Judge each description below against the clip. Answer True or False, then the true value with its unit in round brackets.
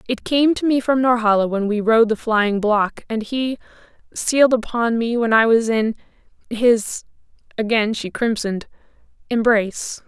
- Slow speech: True (130 wpm)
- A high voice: True (230 Hz)